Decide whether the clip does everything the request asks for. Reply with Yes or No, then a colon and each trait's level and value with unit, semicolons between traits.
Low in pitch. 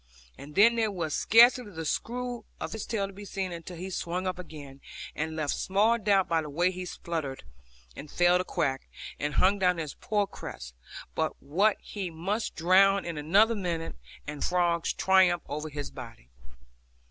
No: medium, 180 Hz